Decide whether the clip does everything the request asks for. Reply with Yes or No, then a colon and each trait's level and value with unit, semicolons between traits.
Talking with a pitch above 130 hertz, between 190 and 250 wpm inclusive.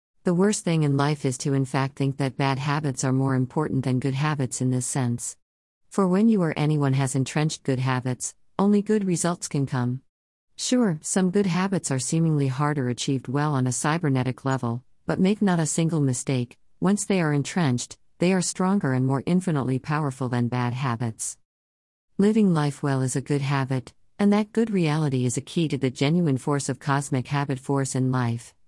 Yes: medium, 140 Hz; average, 195 wpm